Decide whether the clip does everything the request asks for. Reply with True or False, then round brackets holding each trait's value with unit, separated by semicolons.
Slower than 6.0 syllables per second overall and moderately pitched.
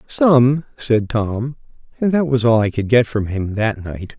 False (4.0 syllables/s; 120 Hz)